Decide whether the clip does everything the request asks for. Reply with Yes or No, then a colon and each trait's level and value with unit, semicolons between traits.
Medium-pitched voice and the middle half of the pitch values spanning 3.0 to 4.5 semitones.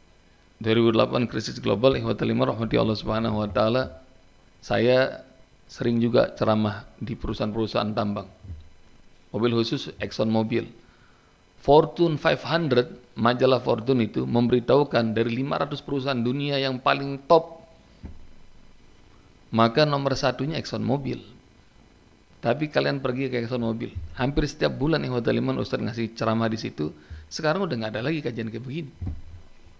No: low, 115 Hz; average, 4.0 semitones